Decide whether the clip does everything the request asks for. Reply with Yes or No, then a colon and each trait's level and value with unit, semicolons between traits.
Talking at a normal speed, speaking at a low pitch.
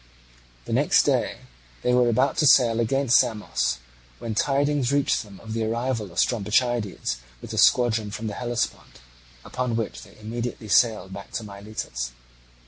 Yes: average, 155 wpm; low, 115 Hz